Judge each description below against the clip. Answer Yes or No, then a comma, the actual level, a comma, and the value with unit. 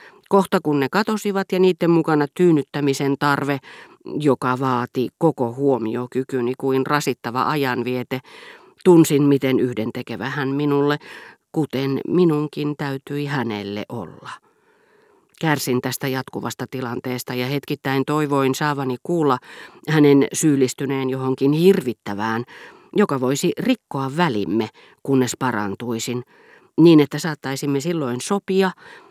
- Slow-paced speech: No, average, 105 wpm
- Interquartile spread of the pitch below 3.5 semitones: No, average, 3.8 semitones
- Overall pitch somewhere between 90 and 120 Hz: No, medium, 140 Hz